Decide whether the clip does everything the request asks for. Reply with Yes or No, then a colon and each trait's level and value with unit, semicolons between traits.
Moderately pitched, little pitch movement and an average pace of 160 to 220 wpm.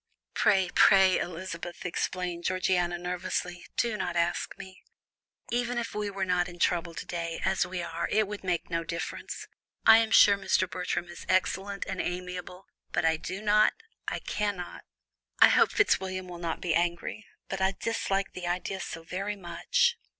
Yes: medium, 180 Hz; narrow, 2.1 semitones; average, 170 wpm